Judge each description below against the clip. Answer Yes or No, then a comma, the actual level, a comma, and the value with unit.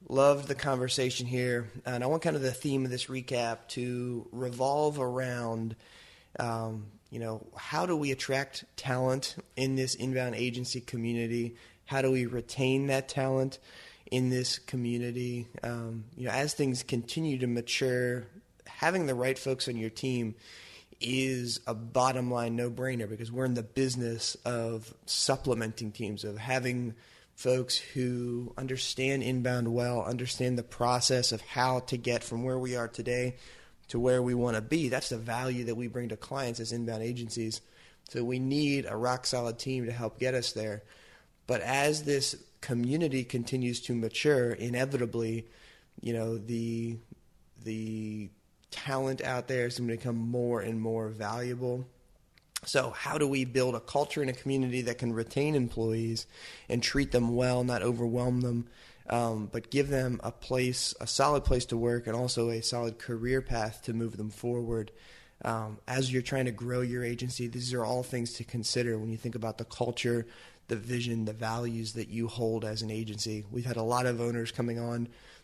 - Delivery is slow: No, average, 175 wpm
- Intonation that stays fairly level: Yes, narrow, 1.8 semitones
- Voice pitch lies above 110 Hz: Yes, low, 120 Hz